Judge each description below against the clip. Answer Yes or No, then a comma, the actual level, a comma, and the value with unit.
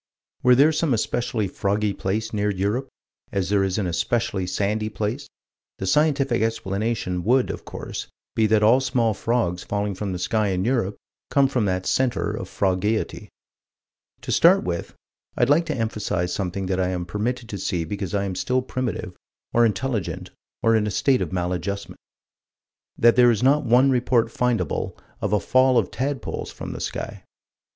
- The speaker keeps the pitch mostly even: No, average, 4.3 semitones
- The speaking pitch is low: Yes, low, 110 Hz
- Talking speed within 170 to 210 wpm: Yes, average, 175 wpm